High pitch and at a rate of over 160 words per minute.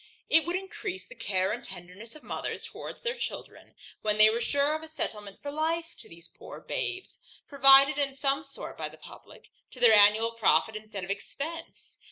Yes: very high, 270 Hz; average, 195 wpm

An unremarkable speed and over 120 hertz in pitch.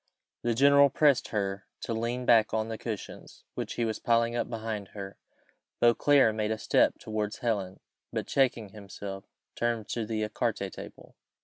No: average, 170 wpm; low, 110 Hz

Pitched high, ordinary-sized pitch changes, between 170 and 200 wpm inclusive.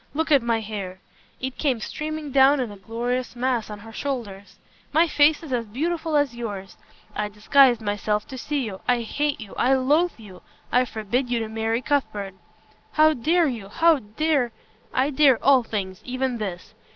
Yes: high, 245 Hz; average, 4.8 semitones; average, 185 wpm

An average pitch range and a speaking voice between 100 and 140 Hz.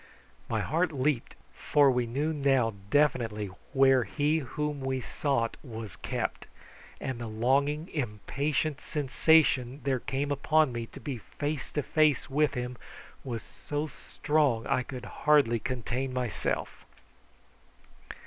Yes: average, 3.3 semitones; low, 135 Hz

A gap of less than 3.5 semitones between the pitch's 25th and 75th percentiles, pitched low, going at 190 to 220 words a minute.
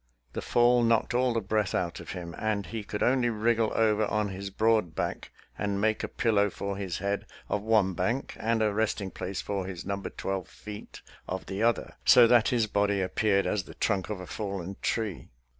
Yes: narrow, 2.4 semitones; low, 105 Hz; fast, 205 wpm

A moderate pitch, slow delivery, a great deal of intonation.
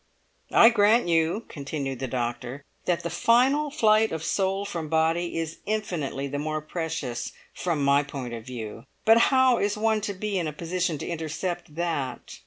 No: medium, 165 Hz; average, 175 wpm; wide, 6.2 semitones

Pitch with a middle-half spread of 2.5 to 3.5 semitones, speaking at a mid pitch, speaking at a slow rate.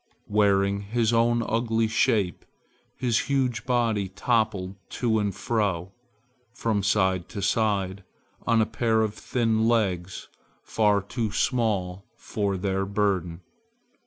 No: average, 2.8 semitones; low, 105 Hz; slow, 120 wpm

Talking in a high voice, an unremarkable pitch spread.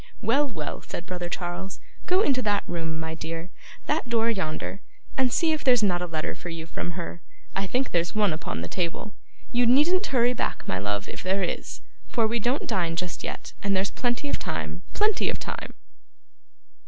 No: high, 195 Hz; wide, 6.5 semitones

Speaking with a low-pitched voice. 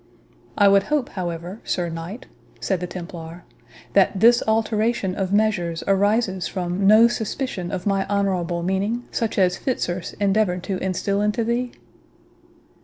No: high, 195 Hz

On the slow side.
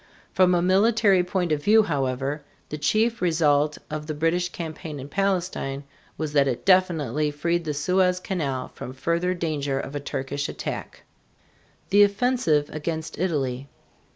No: average, 150 wpm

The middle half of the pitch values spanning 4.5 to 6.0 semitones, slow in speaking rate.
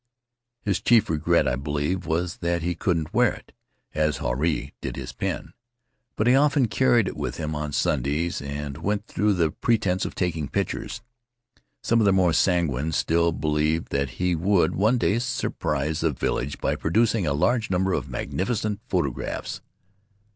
No: average, 5.2 semitones; average, 170 wpm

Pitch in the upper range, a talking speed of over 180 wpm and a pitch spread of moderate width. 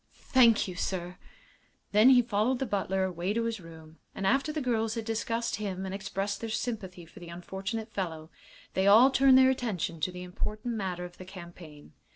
Yes: high, 200 Hz; average, 190 wpm; average, 4.2 semitones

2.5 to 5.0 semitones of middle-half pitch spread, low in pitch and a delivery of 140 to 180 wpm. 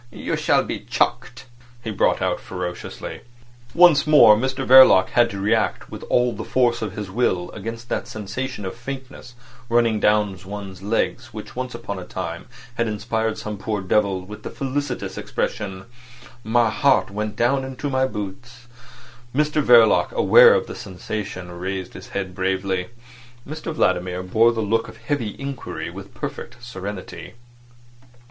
Yes: average, 4.7 semitones; low, 110 Hz; average, 155 wpm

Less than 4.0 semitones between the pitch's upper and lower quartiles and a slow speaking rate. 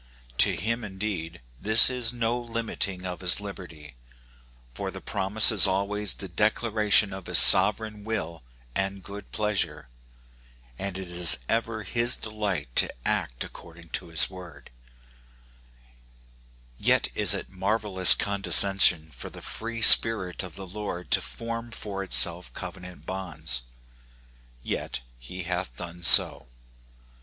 Yes: average, 3.5 semitones; slow, 130 wpm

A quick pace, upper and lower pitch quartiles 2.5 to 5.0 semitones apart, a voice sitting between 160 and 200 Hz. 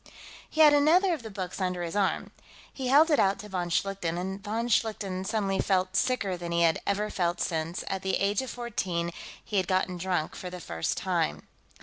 Yes: fast, 210 wpm; average, 3.6 semitones; high, 190 Hz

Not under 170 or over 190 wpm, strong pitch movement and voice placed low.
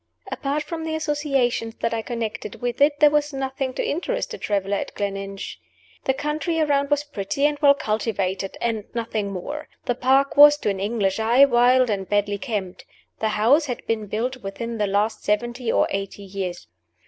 No: average, 185 wpm; wide, 5.7 semitones; high, 235 Hz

